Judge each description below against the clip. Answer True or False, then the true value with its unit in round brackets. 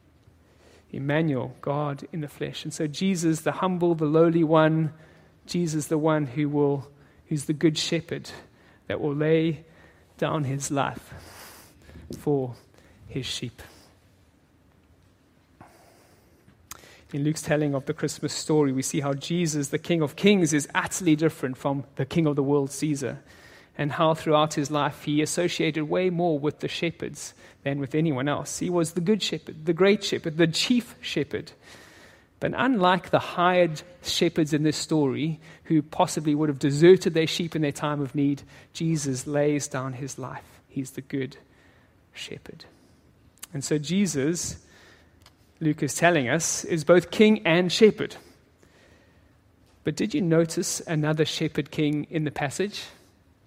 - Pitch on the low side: False (150 Hz)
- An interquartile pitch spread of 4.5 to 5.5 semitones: False (2.9 semitones)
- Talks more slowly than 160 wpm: True (150 wpm)